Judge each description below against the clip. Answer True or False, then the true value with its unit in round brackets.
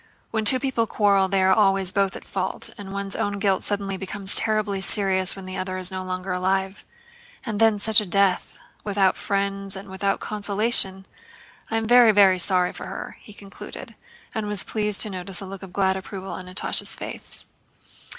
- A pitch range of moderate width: False (1.5 semitones)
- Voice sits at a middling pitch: False (195 Hz)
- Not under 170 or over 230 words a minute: True (190 wpm)